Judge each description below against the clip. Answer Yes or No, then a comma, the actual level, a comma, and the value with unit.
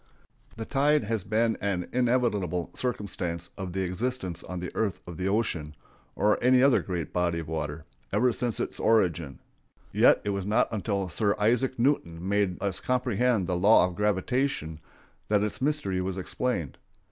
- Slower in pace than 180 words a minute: Yes, average, 170 wpm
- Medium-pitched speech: No, low, 100 Hz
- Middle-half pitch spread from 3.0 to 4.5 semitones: No, average, 5.1 semitones